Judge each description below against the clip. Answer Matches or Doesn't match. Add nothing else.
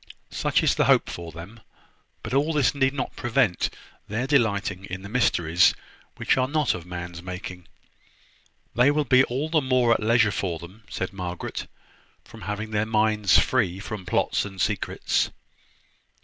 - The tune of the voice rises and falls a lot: Matches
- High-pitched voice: Doesn't match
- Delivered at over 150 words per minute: Matches